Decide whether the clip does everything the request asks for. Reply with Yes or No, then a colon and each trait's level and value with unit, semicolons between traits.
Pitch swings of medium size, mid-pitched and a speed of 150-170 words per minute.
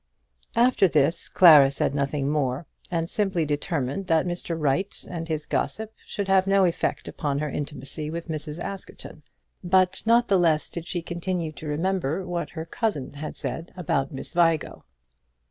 Yes: average, 3.7 semitones; medium, 165 Hz; average, 165 wpm